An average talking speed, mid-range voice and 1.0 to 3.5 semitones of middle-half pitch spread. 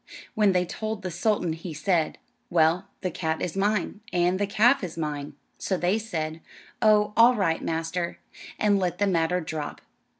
No: average, 170 wpm; medium, 180 Hz; average, 4.0 semitones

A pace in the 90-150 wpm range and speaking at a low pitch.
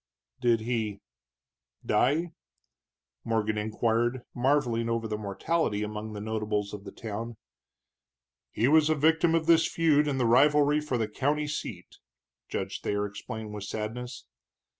Yes: average, 140 wpm; low, 115 Hz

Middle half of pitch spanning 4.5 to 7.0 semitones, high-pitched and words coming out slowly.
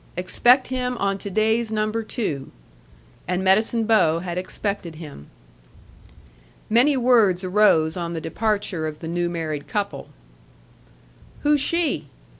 Yes: average, 4.9 semitones; high, 200 Hz; slow, 125 wpm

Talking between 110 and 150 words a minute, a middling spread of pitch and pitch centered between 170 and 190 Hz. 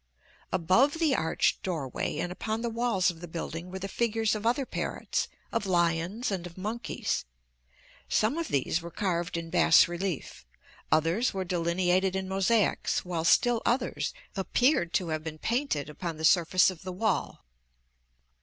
No: average, 160 wpm; average, 4.7 semitones; medium, 185 Hz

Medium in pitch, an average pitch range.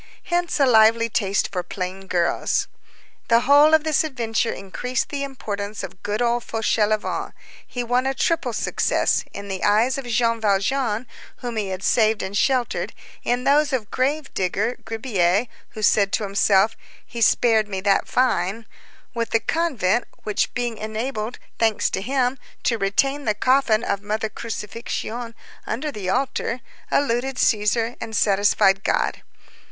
No: high, 225 Hz; average, 3.6 semitones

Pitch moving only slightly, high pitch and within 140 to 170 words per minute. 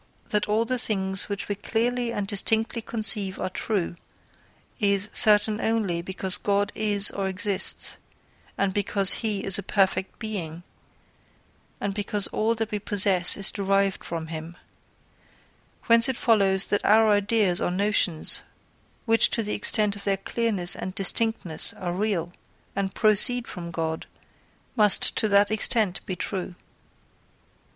Yes: narrow, 2.3 semitones; high, 200 Hz; average, 145 wpm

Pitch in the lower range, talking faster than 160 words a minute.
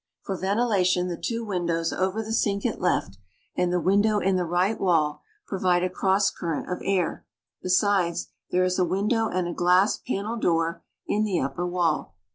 No: medium, 185 Hz; average, 180 wpm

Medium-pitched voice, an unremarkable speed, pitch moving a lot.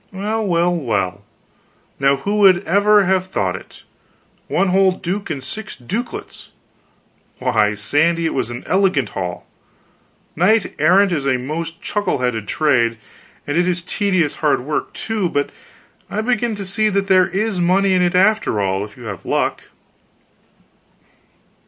Yes: medium, 180 Hz; average, 150 wpm; wide, 6.3 semitones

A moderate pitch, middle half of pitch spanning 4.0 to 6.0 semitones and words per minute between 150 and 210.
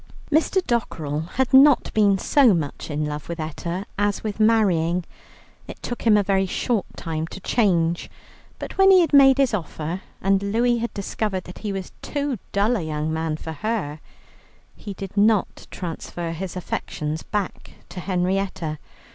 No: high, 195 Hz; average, 5.3 semitones; average, 165 wpm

